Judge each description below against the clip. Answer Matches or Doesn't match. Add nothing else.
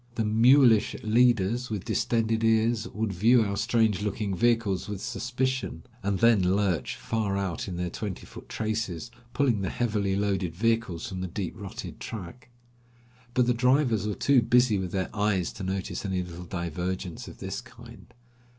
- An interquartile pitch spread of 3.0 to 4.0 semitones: Matches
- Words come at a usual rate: Matches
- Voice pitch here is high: Doesn't match